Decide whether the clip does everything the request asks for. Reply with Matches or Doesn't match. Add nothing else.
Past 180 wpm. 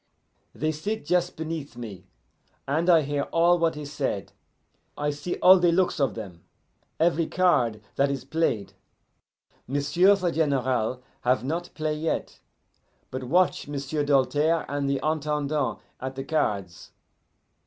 Doesn't match